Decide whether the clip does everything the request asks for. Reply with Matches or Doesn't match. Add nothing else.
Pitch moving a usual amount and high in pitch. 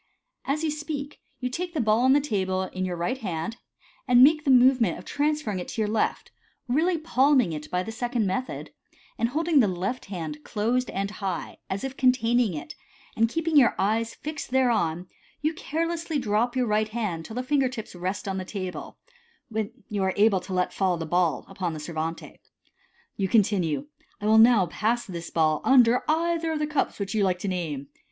Doesn't match